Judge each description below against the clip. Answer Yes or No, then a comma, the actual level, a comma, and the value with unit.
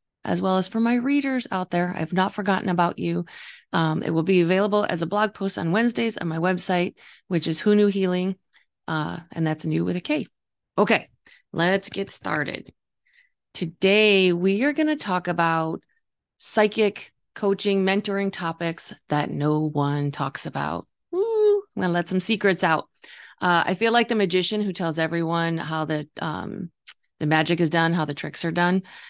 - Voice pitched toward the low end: No, medium, 185 Hz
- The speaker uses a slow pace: No, average, 185 wpm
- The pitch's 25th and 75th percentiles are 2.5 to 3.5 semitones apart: No, average, 4.0 semitones